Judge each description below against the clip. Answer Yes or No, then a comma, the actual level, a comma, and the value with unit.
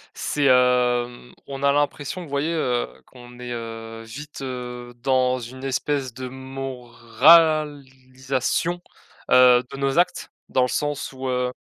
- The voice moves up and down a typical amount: No, narrow, 2.3 semitones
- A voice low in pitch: Yes, low, 130 Hz